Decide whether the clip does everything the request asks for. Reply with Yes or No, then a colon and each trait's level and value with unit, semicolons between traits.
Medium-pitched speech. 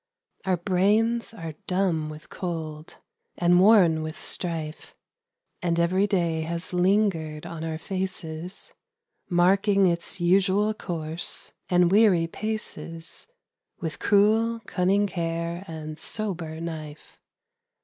Yes: medium, 175 Hz